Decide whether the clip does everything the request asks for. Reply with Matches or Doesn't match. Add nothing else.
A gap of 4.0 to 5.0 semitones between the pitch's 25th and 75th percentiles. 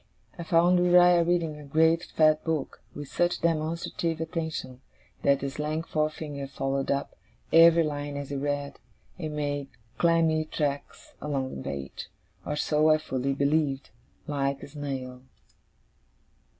Doesn't match